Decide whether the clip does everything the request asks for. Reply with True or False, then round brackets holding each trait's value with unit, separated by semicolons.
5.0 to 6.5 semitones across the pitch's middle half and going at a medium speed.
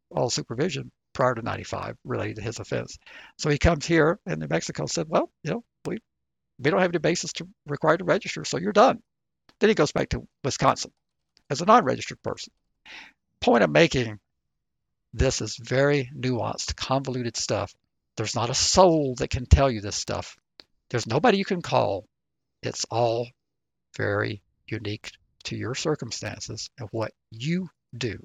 True (5.5 semitones; 170 wpm)